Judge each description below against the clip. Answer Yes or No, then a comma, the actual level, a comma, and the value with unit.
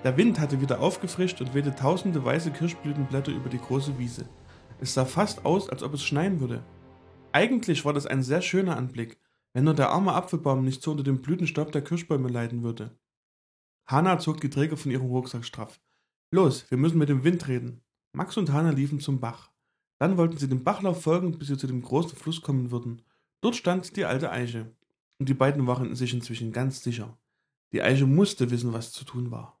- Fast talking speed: Yes, fast, 205 wpm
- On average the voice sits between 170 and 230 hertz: No, medium, 140 Hz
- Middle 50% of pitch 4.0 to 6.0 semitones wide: Yes, average, 4.7 semitones